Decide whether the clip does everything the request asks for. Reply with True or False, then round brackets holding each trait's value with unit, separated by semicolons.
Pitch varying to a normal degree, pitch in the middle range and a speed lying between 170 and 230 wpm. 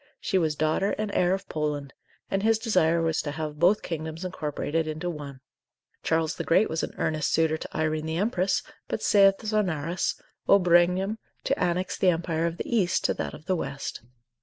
True (3.4 semitones; 170 Hz; 190 wpm)